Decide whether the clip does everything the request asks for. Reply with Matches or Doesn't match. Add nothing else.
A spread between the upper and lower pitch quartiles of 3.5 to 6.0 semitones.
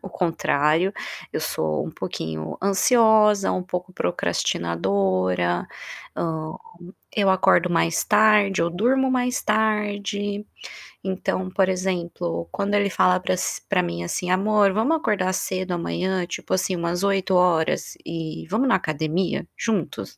Matches